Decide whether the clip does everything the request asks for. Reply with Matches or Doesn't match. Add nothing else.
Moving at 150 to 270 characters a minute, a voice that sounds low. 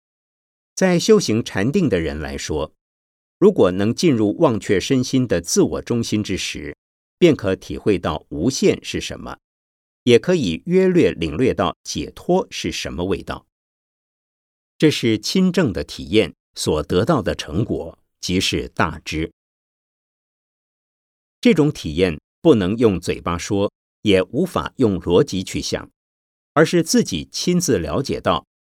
Matches